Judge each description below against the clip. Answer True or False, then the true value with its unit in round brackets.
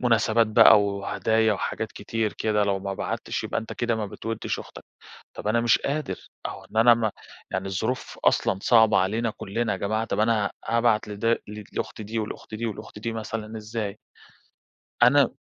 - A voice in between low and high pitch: False (110 Hz)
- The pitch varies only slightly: True (1.8 semitones)